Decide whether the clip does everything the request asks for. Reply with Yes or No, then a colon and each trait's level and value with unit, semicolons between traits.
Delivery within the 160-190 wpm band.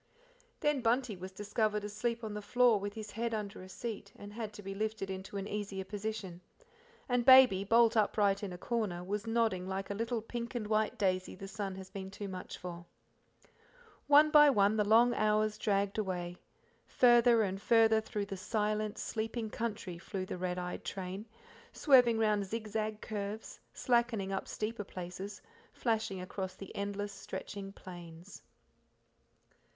Yes: average, 165 wpm